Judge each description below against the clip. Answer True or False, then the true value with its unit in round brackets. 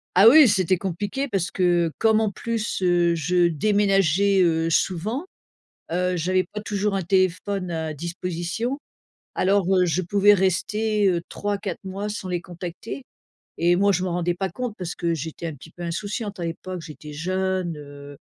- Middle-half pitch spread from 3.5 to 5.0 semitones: False (3.0 semitones)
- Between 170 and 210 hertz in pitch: True (185 Hz)